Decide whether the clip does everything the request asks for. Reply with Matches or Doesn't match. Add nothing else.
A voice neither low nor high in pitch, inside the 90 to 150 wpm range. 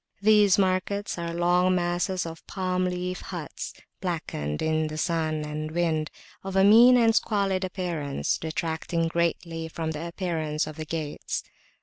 Matches